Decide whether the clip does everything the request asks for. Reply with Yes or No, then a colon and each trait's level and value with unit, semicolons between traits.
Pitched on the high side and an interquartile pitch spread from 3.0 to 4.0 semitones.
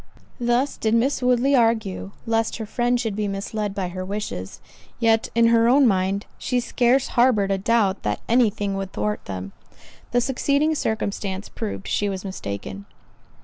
Yes: high, 220 Hz; average, 3.6 semitones